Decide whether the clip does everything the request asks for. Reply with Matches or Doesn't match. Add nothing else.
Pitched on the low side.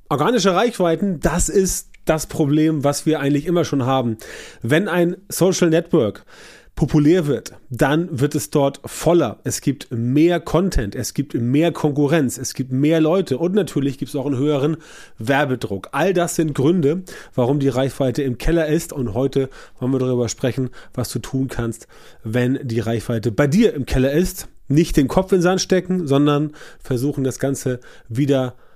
Doesn't match